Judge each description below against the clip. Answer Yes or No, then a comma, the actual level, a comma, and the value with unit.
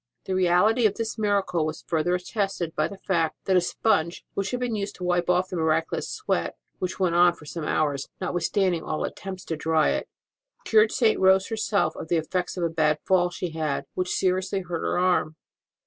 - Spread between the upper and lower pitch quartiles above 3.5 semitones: No, average, 3.0 semitones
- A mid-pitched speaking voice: Yes, medium, 180 Hz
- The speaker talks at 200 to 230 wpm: Yes, fast, 205 wpm